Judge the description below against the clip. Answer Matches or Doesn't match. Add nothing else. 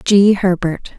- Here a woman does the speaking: Matches